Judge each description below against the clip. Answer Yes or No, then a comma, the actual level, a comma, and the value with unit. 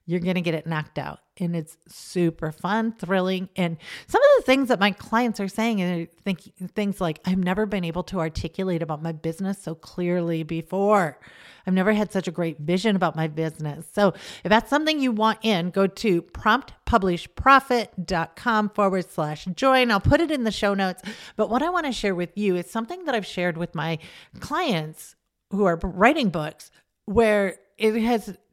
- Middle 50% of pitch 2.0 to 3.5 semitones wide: No, average, 4.4 semitones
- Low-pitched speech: No, high, 190 Hz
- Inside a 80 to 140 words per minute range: No, average, 190 wpm